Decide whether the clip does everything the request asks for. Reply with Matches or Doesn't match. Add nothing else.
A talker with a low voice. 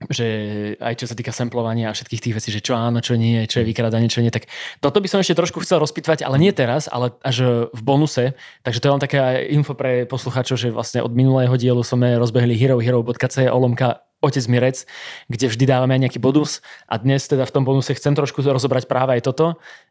Matches